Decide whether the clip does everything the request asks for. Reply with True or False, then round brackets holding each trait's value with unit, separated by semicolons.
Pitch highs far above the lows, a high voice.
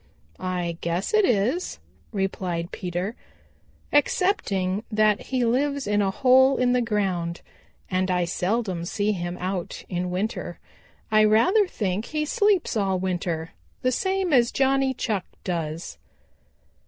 True (6.0 semitones; 205 Hz)